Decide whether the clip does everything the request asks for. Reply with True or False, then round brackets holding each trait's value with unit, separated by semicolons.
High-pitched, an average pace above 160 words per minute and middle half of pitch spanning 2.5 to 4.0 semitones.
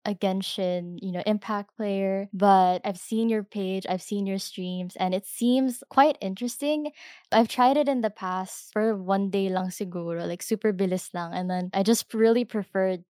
True (195 Hz; 190 wpm; 3.3 semitones)